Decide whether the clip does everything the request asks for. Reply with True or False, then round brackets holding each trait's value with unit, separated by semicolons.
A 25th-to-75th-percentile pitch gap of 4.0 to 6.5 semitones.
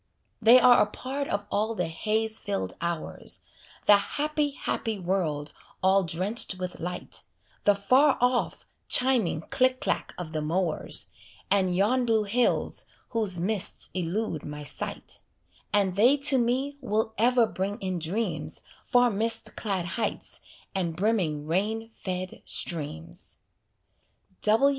True (4.6 semitones)